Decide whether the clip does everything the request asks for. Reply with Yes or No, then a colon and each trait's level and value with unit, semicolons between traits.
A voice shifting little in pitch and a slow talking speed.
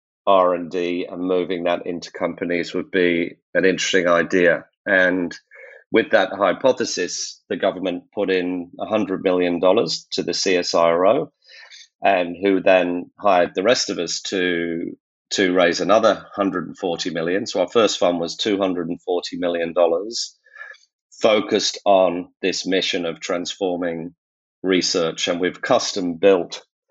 Yes: narrow, 1.3 semitones; slow, 130 wpm